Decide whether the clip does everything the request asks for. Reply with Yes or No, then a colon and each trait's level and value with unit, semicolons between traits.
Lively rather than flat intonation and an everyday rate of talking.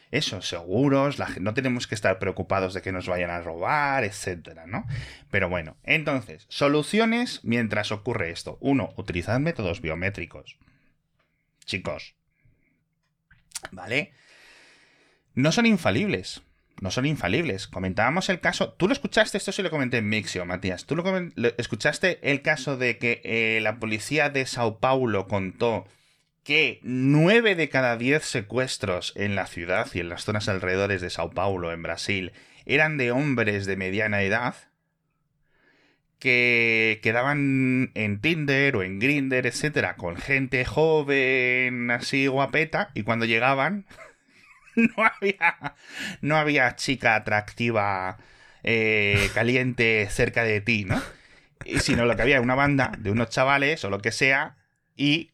Yes: wide, 5.9 semitones; average, 145 wpm